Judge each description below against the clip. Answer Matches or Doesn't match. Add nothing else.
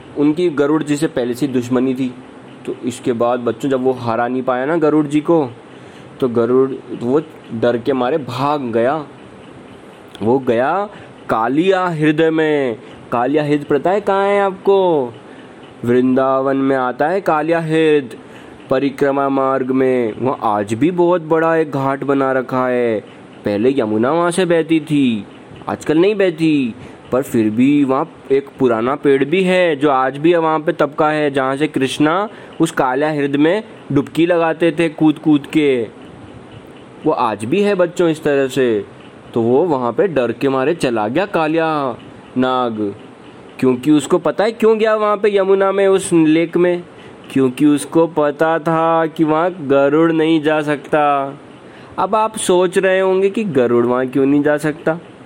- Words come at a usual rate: Matches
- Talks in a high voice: Doesn't match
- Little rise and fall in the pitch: Doesn't match